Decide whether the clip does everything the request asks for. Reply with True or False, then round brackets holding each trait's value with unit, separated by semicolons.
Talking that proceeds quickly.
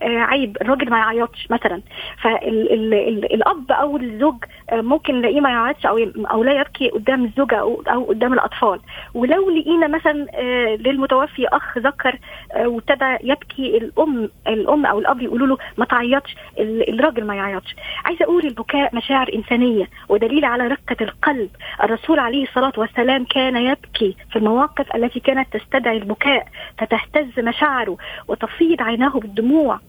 True (150 wpm)